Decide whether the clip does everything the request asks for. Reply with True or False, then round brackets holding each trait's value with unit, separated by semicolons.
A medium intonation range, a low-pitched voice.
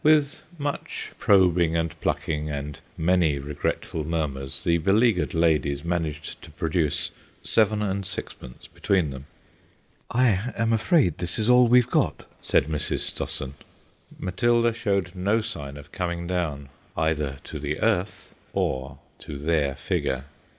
False (5.9 semitones; 85 Hz)